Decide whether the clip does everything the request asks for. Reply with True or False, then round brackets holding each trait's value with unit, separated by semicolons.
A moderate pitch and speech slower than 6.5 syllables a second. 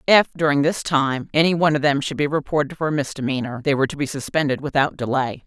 False (145 Hz; 6.6 syllables/s)